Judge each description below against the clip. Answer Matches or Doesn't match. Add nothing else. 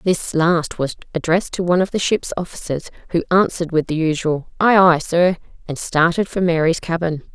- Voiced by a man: Doesn't match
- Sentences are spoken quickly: Doesn't match